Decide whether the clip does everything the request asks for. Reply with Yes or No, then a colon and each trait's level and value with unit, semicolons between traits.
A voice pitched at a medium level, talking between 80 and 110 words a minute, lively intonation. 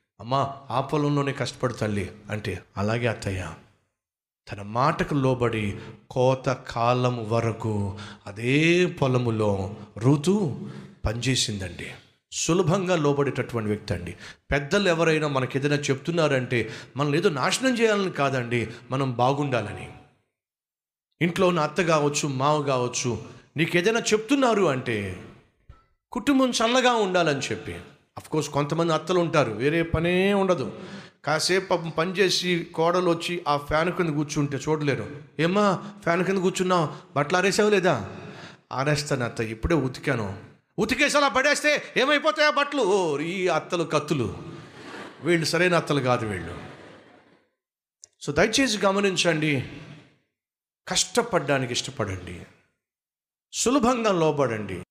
Yes: medium, 145 Hz; average, 100 wpm; wide, 7.1 semitones